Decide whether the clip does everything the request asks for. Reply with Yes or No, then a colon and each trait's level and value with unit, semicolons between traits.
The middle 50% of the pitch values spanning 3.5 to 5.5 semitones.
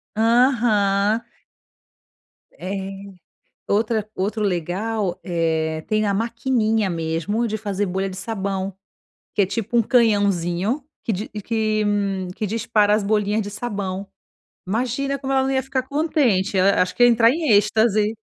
No: average, 3.0 semitones